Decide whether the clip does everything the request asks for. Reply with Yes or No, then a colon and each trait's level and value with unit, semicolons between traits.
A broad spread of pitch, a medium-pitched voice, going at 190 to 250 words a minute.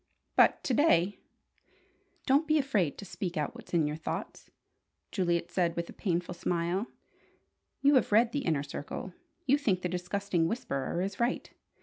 No: wide, 5.7 semitones; medium, 180 Hz; average, 165 wpm